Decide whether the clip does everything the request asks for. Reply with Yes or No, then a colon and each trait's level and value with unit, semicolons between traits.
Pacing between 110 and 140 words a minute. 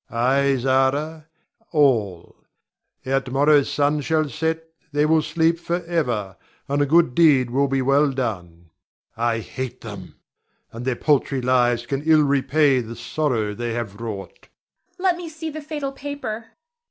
No: average, 155 wpm